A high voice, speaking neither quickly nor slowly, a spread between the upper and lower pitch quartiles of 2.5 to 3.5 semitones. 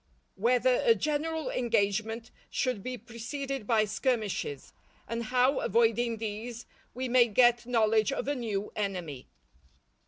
No: high, 235 Hz; slow, 125 wpm; average, 2.8 semitones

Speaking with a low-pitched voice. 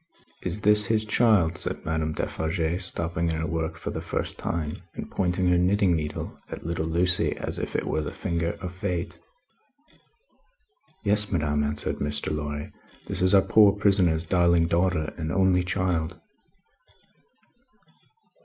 Yes: very low, 85 Hz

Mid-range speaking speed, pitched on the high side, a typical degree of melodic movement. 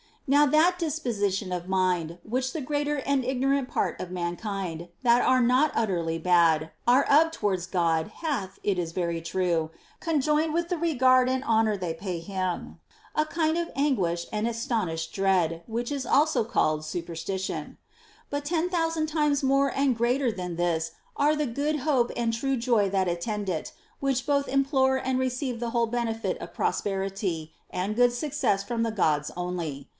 No: average, 170 wpm; high, 230 Hz; wide, 7.5 semitones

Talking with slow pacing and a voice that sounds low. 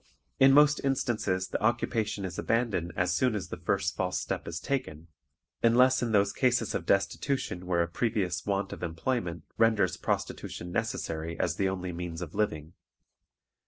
No: average, 160 wpm; low, 100 Hz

